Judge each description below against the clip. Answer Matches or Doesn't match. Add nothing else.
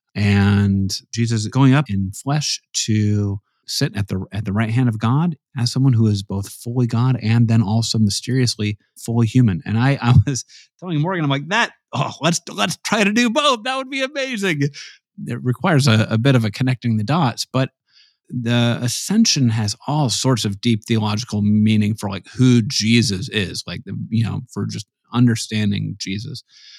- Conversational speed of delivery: Matches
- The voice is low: Matches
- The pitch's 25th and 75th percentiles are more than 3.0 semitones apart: Matches